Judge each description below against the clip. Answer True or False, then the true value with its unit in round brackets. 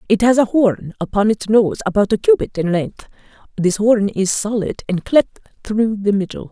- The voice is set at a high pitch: True (210 Hz)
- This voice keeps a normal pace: True (195 wpm)